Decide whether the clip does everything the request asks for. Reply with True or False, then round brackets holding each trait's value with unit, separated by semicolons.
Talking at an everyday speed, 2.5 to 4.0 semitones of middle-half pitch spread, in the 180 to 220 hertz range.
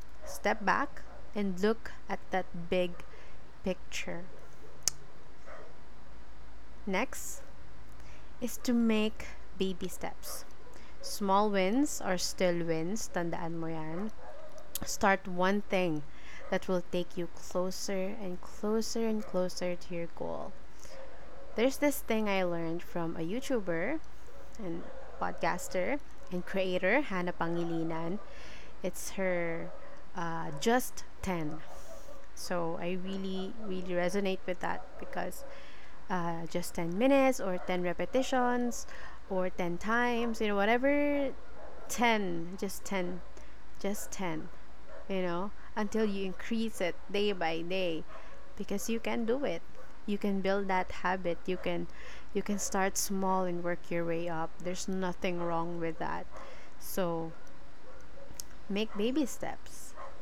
True (120 wpm; 3.6 semitones; 190 Hz)